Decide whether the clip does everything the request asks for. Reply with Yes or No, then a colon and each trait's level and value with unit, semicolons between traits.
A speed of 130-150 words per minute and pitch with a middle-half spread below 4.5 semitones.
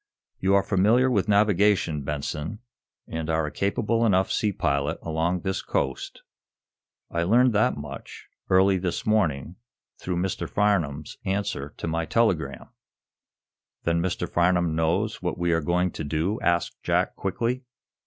Yes: average, 145 wpm; average, 4.0 semitones